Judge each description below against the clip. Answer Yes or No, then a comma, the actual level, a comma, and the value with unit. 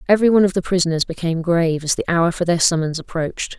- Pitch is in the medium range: Yes, medium, 170 Hz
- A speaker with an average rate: No, fast, 235 wpm